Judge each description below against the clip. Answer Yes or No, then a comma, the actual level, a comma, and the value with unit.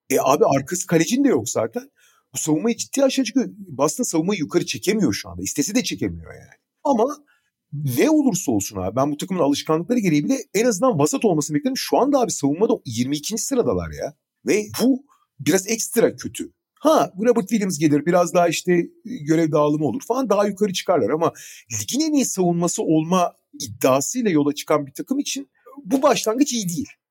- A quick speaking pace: Yes, fast, 175 wpm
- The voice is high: Yes, high, 200 Hz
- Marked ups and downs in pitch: Yes, wide, 8.7 semitones